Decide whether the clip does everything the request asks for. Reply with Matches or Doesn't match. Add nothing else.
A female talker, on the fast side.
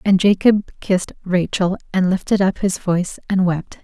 Doesn't match